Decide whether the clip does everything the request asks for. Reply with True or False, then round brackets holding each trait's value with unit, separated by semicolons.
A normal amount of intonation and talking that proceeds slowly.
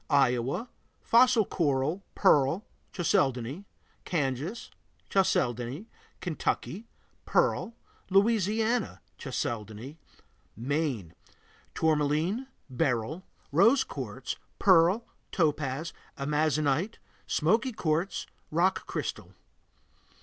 False (6.5 semitones; 70 wpm)